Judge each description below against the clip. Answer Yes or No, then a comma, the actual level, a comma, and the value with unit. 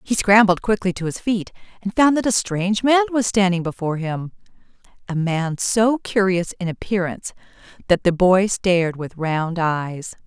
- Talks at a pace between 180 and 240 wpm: No, average, 165 wpm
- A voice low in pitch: No, high, 190 Hz